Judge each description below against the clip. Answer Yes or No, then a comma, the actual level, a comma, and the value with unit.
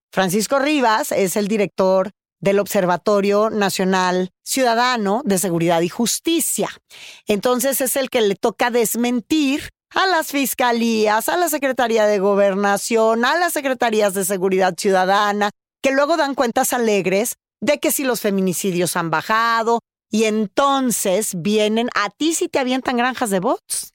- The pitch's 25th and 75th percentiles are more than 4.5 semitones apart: Yes, average, 4.9 semitones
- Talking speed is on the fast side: No, average, 145 wpm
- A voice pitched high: Yes, high, 220 Hz